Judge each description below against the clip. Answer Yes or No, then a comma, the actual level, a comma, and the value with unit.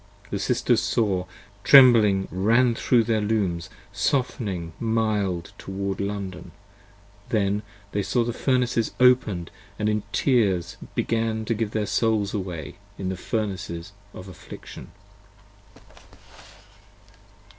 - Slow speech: Yes, slow, 115 wpm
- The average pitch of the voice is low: Yes, low, 105 Hz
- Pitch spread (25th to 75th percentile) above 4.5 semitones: No, average, 3.1 semitones